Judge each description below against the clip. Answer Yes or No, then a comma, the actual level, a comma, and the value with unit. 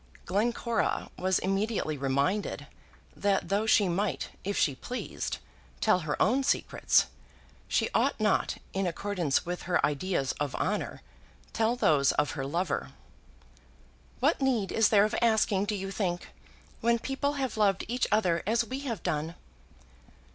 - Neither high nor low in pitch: No, high, 195 Hz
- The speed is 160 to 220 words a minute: No, average, 145 wpm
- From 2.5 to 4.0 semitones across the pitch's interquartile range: No, average, 4.7 semitones